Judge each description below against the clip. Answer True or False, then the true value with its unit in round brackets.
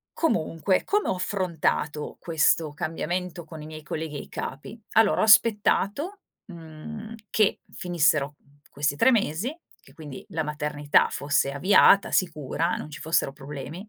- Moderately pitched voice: True (160 Hz)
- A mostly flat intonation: False (5.0 semitones)